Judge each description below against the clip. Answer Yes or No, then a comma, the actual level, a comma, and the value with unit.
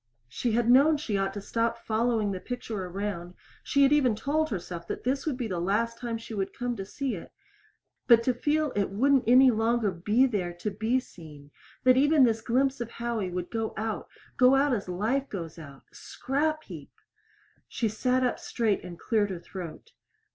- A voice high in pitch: Yes, high, 230 Hz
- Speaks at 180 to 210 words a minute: Yes, average, 190 wpm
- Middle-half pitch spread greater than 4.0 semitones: Yes, average, 4.7 semitones